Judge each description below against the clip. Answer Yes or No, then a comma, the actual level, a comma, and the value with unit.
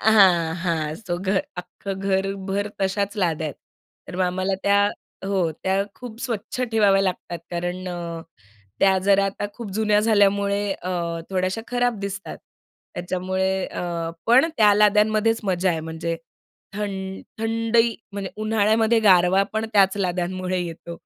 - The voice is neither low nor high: No, high, 195 Hz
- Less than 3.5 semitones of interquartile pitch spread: Yes, narrow, 2.6 semitones